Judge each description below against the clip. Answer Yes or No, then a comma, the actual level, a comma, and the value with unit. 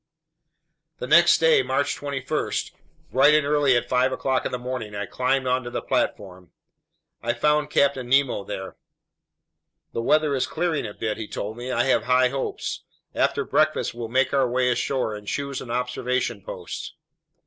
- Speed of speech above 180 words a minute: No, average, 170 wpm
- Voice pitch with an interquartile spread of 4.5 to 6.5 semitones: No, average, 2.7 semitones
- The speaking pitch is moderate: No, low, 125 Hz